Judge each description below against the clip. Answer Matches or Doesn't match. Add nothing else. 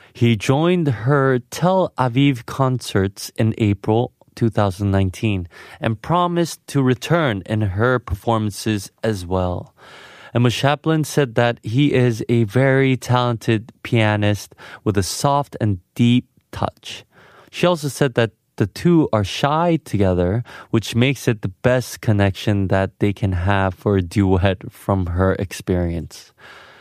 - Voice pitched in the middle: Doesn't match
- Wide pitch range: Doesn't match